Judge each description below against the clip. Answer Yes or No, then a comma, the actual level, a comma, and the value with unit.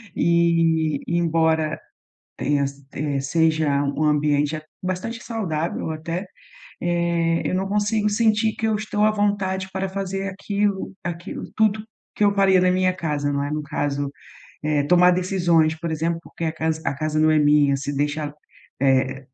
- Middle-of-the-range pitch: Yes, medium, 165 Hz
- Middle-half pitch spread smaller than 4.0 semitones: No, average, 4.3 semitones